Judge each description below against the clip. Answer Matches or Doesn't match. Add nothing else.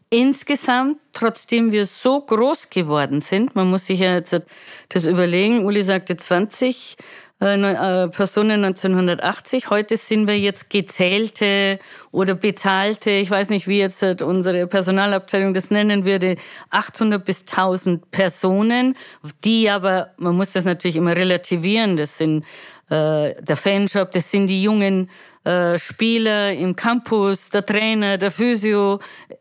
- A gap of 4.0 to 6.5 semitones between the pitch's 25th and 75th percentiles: Doesn't match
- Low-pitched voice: Doesn't match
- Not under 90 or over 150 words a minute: Matches